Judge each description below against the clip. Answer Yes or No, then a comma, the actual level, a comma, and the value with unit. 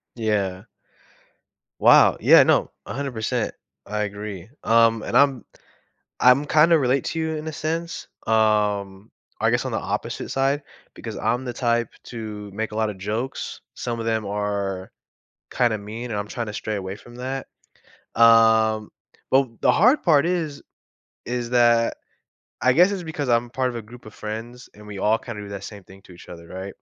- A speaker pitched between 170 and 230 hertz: No, low, 115 Hz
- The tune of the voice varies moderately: Yes, average, 3.6 semitones